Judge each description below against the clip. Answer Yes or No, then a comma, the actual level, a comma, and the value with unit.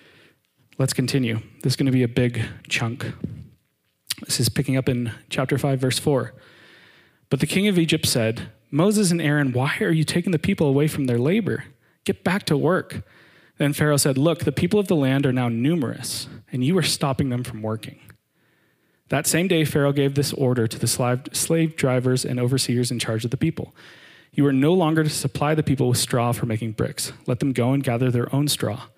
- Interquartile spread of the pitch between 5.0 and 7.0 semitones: No, average, 3.7 semitones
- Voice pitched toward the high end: No, low, 135 Hz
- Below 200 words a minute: No, fast, 205 wpm